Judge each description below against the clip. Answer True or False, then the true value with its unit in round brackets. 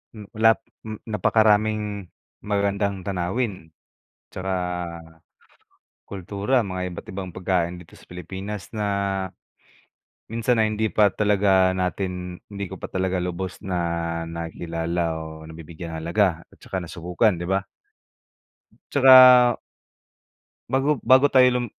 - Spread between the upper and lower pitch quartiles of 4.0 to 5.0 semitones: False (3.5 semitones)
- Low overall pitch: True (95 Hz)